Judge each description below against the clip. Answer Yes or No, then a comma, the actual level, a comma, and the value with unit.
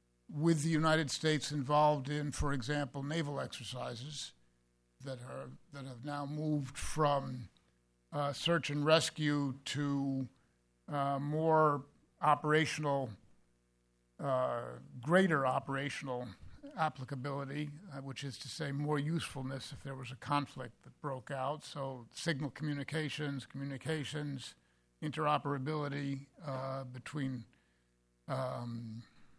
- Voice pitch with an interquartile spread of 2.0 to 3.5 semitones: Yes, average, 2.8 semitones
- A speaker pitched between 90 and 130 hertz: No, medium, 140 Hz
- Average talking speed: No, slow, 105 wpm